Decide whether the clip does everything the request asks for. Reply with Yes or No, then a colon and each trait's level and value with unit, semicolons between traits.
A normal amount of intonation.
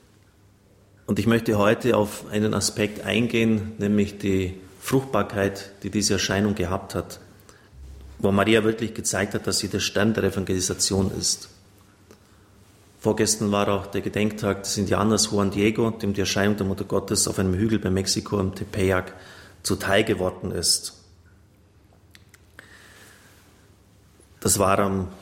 No: narrow, 1.5 semitones